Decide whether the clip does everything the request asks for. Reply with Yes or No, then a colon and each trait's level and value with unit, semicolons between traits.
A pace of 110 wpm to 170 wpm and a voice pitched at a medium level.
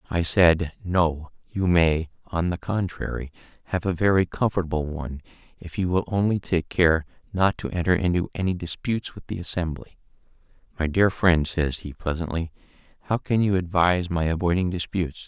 No: average, 160 wpm; very low, 85 Hz